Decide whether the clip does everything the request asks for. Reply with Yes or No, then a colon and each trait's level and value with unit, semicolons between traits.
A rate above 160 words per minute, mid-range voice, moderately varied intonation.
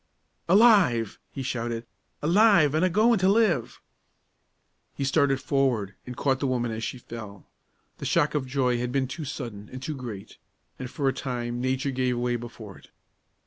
No: average, 175 wpm; low, 130 Hz; average, 3.5 semitones